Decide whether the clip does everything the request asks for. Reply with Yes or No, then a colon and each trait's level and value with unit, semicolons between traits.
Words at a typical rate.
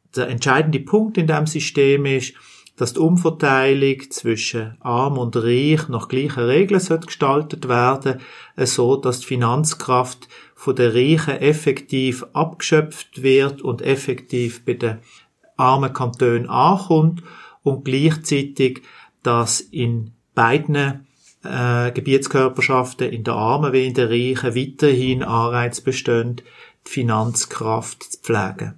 No: slow, 115 wpm